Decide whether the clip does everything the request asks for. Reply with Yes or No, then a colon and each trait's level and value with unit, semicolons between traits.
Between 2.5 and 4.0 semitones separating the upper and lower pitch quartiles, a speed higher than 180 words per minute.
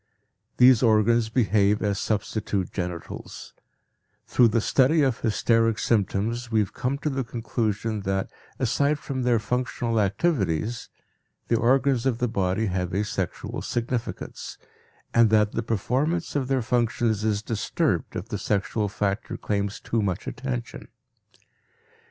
No: average, 3.2 semitones; slow, 135 wpm